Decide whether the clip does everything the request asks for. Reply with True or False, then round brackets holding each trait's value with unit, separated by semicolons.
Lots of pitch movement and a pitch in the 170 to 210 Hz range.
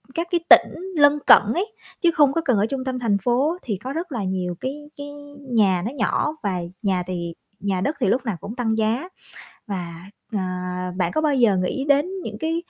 False (6.6 semitones; 240 Hz)